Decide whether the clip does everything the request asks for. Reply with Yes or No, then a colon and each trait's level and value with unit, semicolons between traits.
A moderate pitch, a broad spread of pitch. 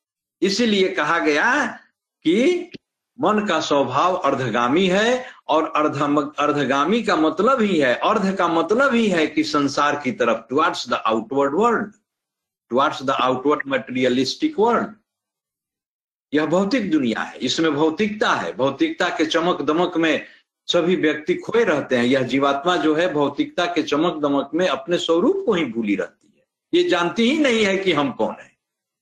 Yes: medium, 170 Hz; wide, 6.6 semitones